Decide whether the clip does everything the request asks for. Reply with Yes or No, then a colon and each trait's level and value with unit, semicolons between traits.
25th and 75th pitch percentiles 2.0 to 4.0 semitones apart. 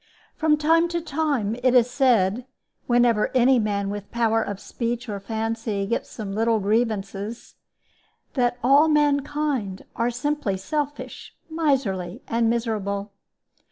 No: average, 5.0 semitones